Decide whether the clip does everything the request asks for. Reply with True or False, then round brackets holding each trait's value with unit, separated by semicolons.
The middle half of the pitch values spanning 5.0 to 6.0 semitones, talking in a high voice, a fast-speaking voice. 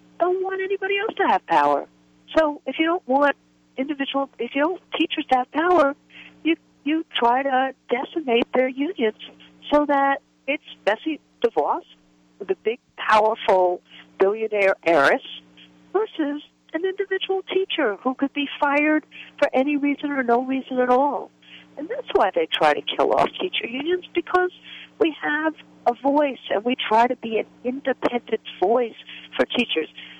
False (5.4 semitones; 275 Hz; 155 wpm)